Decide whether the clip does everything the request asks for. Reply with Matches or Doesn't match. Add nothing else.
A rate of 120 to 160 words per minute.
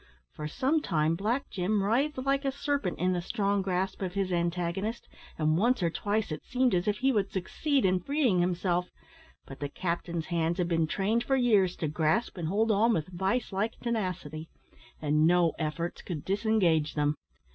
Doesn't match